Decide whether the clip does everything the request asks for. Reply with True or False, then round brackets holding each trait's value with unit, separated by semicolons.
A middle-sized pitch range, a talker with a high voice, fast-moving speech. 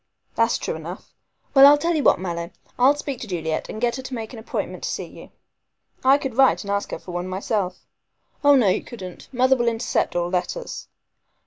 False (6.4 semitones; 235 Hz; 215 wpm)